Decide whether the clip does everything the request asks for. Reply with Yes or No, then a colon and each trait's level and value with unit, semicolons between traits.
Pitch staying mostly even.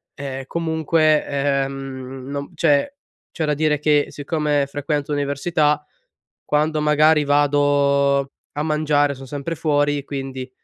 Yes: narrow, 1.5 semitones